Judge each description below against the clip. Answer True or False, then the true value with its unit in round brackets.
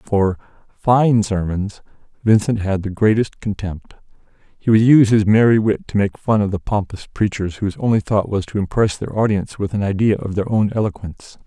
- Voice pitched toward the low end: True (100 Hz)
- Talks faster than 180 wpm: True (190 wpm)